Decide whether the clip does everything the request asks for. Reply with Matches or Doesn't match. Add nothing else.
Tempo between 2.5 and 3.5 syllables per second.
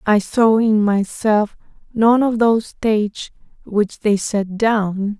Matches